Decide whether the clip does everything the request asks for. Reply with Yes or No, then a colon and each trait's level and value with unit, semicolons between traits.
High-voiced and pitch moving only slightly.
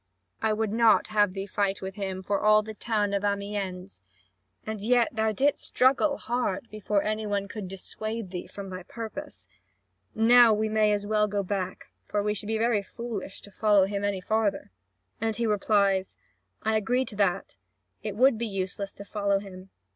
Yes: high, 210 Hz; narrow, 1.9 semitones